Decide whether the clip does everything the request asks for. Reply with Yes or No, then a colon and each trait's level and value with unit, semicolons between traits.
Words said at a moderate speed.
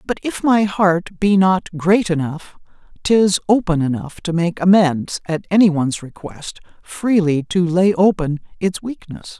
Yes: average, 155 wpm